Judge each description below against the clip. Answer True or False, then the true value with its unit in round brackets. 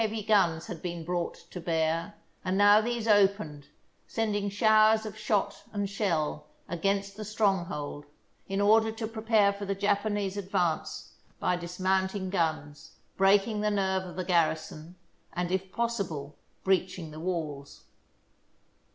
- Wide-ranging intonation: False (3.3 semitones)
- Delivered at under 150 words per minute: True (140 wpm)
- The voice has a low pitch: False (195 Hz)